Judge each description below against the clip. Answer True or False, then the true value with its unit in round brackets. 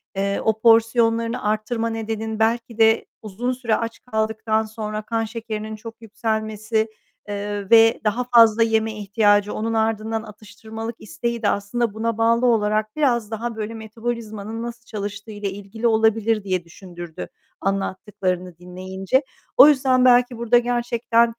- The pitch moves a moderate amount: False (1.7 semitones)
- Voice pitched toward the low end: False (220 Hz)